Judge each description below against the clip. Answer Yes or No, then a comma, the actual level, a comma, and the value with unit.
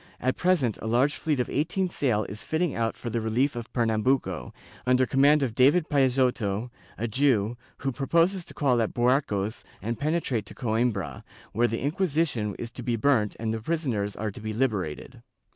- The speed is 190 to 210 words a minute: No, average, 180 wpm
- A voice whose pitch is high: No, low, 120 Hz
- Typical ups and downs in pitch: Yes, average, 4.3 semitones